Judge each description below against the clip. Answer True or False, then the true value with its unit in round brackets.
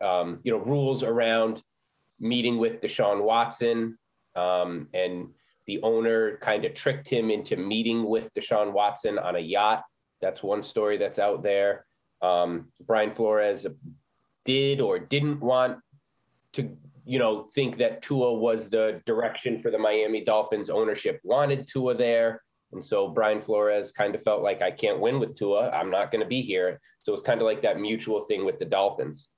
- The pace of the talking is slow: False (175 wpm)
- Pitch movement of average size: True (4.2 semitones)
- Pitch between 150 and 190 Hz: False (115 Hz)